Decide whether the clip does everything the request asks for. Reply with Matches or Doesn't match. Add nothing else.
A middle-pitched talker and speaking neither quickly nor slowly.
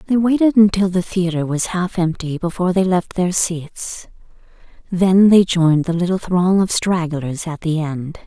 Matches